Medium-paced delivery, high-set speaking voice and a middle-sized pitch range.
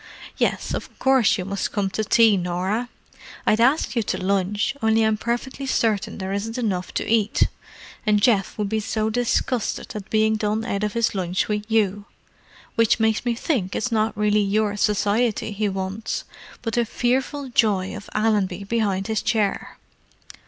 No: average, 170 wpm; high, 215 Hz; narrow, 2.3 semitones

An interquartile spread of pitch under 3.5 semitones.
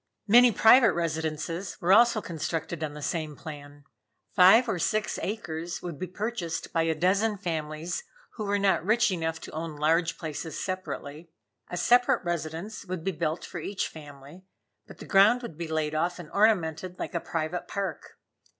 No: average, 4.0 semitones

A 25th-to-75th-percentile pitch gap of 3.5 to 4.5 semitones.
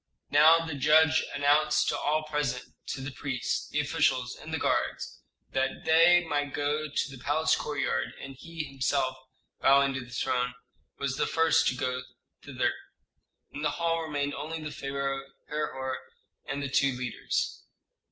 No: narrow, 2.4 semitones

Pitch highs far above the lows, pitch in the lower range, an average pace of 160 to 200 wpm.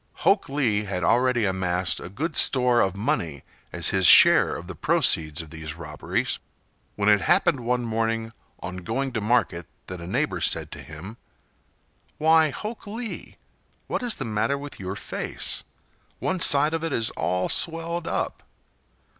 Yes: wide, 7.6 semitones; low, 115 Hz; average, 165 wpm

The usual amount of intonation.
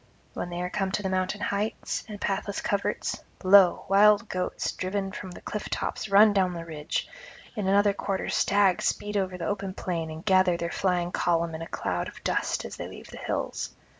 No: narrow, 2.2 semitones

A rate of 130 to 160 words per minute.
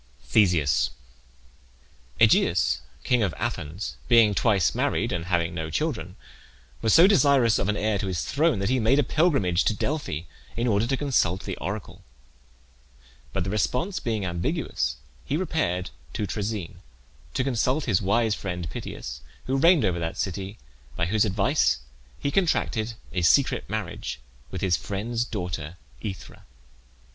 Yes: average, 150 wpm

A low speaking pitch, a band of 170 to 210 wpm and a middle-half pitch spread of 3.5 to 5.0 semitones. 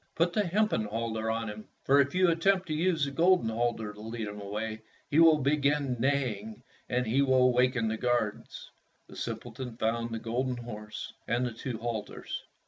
Yes: low, 120 Hz; average, 185 wpm; average, 4.1 semitones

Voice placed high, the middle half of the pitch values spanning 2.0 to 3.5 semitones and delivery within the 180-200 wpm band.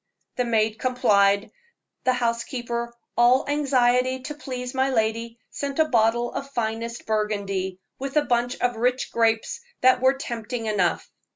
No: high, 240 Hz; narrow, 2.5 semitones; average, 145 wpm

